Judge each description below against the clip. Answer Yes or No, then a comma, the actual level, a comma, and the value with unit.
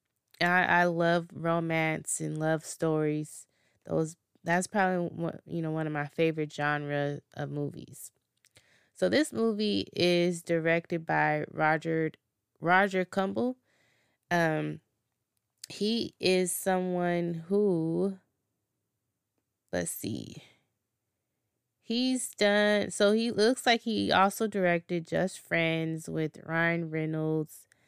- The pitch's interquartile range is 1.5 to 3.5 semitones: Yes, average, 3.1 semitones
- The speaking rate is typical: No, slow, 110 wpm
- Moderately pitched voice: Yes, medium, 165 Hz